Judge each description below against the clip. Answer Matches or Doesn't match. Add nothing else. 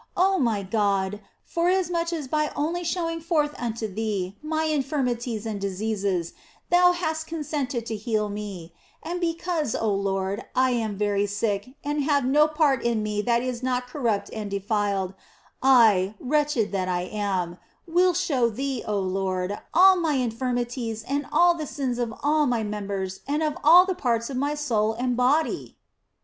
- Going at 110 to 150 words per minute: Doesn't match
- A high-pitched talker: Matches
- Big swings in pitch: Matches